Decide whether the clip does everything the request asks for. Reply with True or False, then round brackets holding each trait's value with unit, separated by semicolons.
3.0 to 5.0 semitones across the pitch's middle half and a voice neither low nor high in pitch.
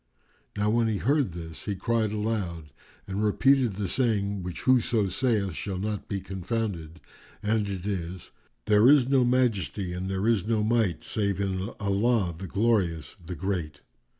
False (3.4 semitones; 100 Hz)